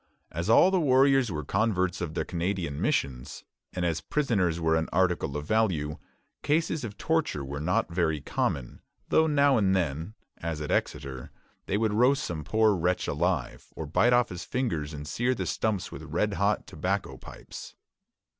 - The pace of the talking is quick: No, average, 175 wpm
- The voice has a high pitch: No, very low, 90 Hz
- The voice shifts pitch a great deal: Yes, wide, 6.6 semitones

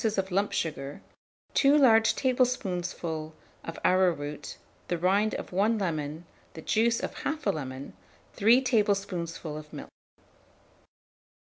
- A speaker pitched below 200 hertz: Yes, medium, 185 Hz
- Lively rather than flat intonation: Yes, wide, 5.8 semitones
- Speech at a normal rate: No, slow, 115 wpm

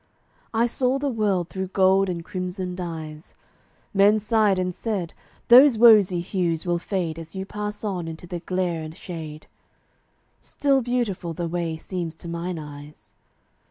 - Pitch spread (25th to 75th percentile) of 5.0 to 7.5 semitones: No, average, 3.7 semitones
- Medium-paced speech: Yes, average, 155 wpm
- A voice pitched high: No, medium, 180 Hz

